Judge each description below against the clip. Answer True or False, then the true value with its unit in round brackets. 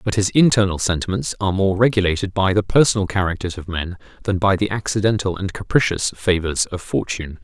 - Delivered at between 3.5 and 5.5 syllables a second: False (6.0 syllables/s)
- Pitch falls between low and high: False (95 Hz)